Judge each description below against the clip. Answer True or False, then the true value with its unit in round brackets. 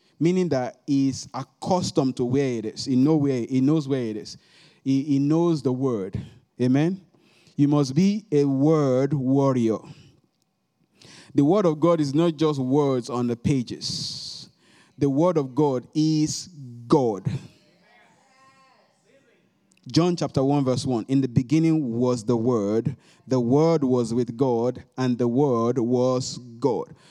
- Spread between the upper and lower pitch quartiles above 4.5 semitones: False (3.8 semitones)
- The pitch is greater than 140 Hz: False (135 Hz)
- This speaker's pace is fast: False (145 wpm)